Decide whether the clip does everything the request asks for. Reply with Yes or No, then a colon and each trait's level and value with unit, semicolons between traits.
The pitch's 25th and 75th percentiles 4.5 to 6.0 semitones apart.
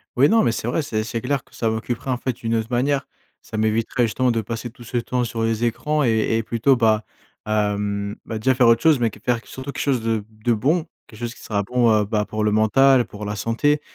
No: narrow, 2.6 semitones